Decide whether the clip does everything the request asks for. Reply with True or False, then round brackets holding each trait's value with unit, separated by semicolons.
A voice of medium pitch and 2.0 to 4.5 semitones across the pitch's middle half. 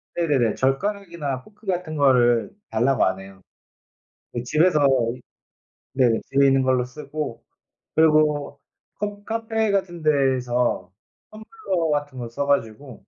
False (145 Hz; 5.6 semitones)